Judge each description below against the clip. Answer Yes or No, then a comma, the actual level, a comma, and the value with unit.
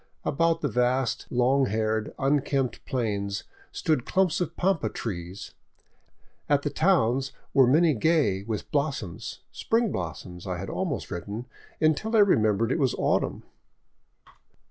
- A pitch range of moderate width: No, wide, 6.6 semitones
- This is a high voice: No, low, 130 Hz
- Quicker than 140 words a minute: No, slow, 135 wpm